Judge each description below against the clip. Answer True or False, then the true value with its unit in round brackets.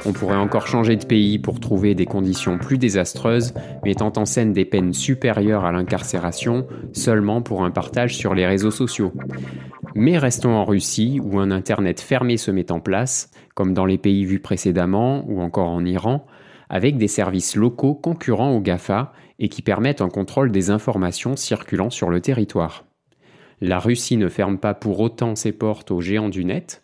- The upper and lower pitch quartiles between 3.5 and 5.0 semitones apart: True (4.1 semitones)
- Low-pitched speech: True (105 Hz)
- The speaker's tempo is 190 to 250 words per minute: False (180 wpm)